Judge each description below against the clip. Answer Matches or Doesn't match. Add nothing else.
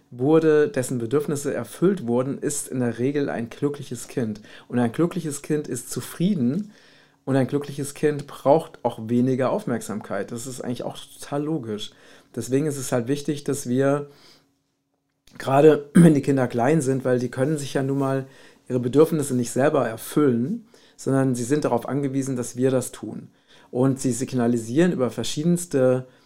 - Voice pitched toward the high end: Doesn't match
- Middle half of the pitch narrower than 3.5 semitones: Matches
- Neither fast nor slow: Matches